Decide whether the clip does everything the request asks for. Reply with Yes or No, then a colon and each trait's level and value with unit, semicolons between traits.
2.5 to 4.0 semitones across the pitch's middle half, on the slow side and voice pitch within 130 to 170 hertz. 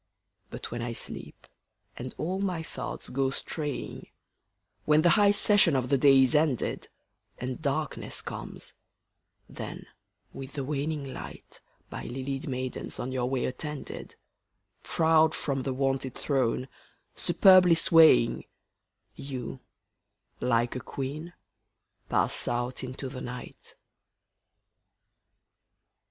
Yes: average, 3.5 semitones; slow, 115 wpm; low, 135 Hz